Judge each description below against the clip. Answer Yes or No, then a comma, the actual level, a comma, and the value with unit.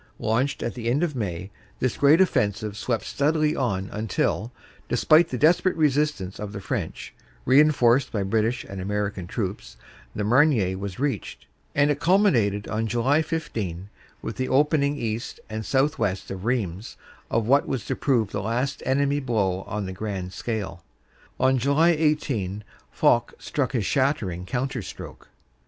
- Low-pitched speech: Yes, low, 120 Hz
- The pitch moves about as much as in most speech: No, wide, 5.8 semitones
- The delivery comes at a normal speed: Yes, average, 160 wpm